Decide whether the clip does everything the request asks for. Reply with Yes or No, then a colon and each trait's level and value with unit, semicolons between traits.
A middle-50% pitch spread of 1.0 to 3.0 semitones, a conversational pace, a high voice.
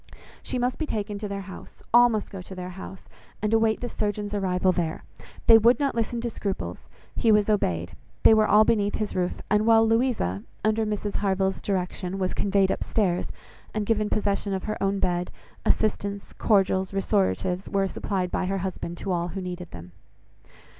Yes: narrow, 2.6 semitones; average, 190 wpm; high, 200 Hz